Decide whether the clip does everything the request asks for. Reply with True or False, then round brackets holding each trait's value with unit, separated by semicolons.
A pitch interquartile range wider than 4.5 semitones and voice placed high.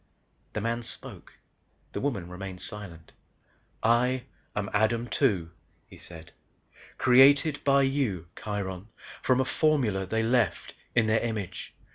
False (5.0 semitones; 110 Hz)